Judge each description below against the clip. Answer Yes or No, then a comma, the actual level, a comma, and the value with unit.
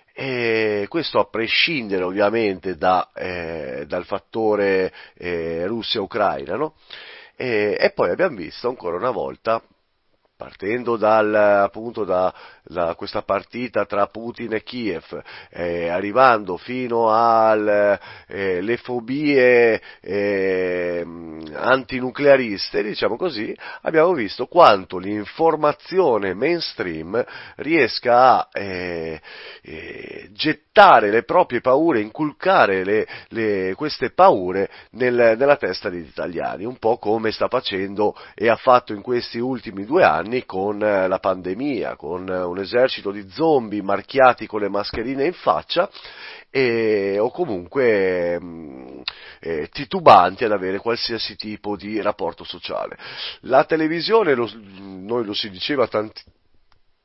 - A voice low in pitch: Yes, low, 105 Hz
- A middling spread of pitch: Yes, average, 4.4 semitones